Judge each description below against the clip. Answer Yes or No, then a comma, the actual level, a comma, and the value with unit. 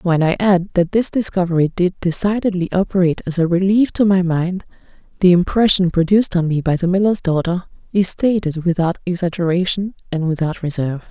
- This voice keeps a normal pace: Yes, average, 165 wpm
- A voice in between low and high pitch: Yes, medium, 180 Hz